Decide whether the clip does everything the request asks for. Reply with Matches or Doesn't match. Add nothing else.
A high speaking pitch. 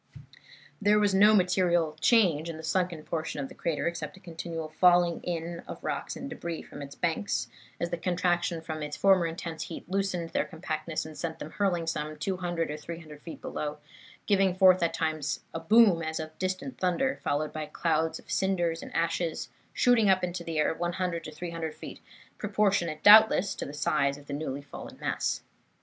Doesn't match